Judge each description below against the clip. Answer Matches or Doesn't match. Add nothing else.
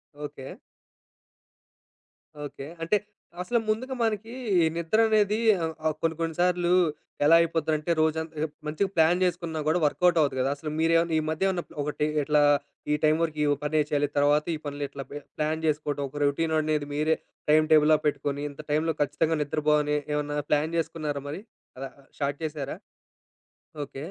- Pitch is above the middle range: Doesn't match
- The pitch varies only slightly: Matches